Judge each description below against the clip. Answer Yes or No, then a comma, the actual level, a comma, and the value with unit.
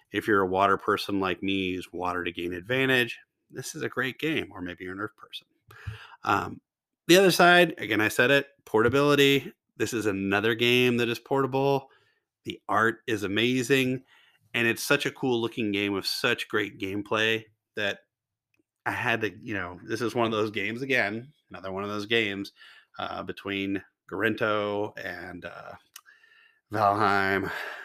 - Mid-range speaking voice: No, low, 115 Hz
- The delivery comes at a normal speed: Yes, average, 170 wpm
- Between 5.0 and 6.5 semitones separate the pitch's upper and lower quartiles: Yes, average, 5.3 semitones